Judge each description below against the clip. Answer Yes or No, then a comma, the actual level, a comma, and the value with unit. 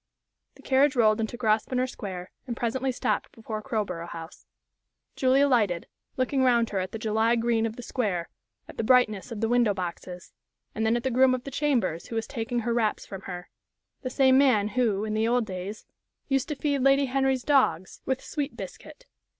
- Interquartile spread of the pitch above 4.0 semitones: No, average, 3.6 semitones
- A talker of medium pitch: No, high, 230 Hz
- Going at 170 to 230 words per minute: Yes, average, 195 wpm